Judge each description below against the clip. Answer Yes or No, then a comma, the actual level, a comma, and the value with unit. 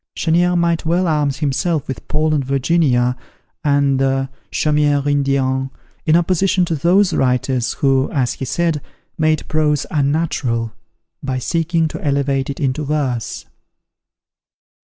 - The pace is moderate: No, slow, 130 wpm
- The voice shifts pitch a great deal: No, average, 3.3 semitones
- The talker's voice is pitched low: No, medium, 145 Hz